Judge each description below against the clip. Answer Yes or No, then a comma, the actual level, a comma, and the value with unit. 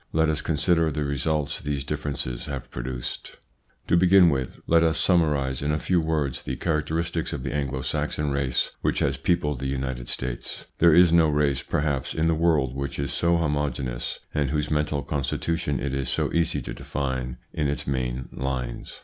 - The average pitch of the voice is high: No, very low, 75 Hz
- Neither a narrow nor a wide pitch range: Yes, average, 3.1 semitones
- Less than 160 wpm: No, average, 185 wpm